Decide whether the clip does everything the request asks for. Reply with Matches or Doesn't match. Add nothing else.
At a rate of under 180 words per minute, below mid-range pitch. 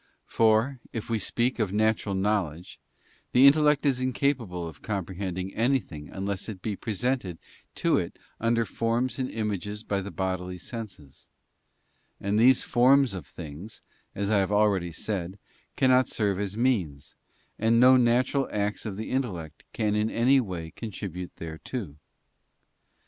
Matches